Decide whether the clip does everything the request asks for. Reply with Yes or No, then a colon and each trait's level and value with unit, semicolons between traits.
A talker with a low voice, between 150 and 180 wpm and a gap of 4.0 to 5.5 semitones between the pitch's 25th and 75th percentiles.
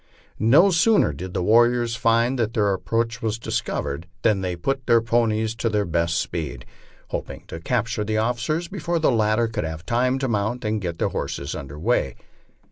No: low, 110 Hz; average, 190 wpm; average, 4.4 semitones